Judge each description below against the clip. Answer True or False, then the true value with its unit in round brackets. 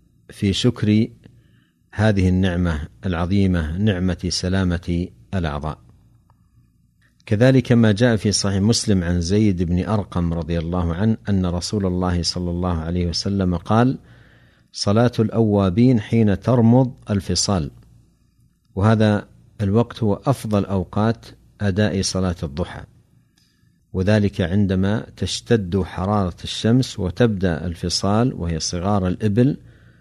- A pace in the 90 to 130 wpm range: True (105 wpm)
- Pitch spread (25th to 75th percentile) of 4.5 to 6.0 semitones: False (3.7 semitones)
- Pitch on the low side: True (100 Hz)